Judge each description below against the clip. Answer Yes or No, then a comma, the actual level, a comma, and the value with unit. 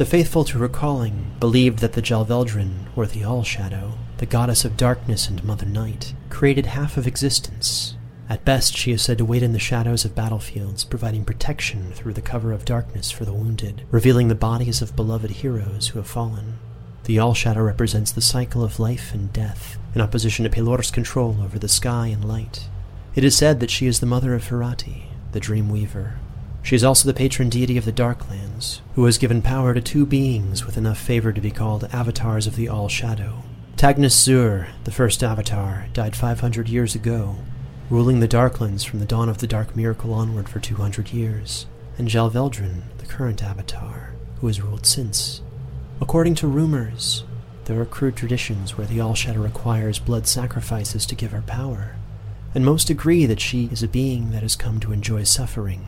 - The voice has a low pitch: Yes, low, 115 Hz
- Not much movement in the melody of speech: Yes, narrow, 2.3 semitones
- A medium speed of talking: Yes, average, 190 wpm